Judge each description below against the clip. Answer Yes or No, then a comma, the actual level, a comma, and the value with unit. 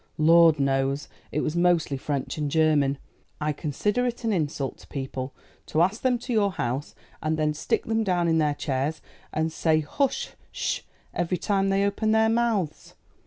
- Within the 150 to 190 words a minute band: Yes, average, 180 wpm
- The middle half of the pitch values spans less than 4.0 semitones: No, wide, 5.5 semitones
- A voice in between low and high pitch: Yes, medium, 160 Hz